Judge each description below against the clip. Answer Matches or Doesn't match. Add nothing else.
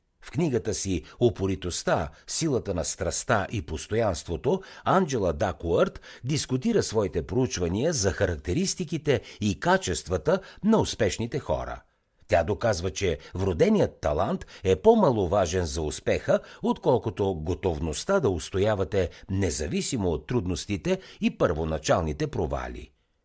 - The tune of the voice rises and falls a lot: Matches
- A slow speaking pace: Matches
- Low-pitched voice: Matches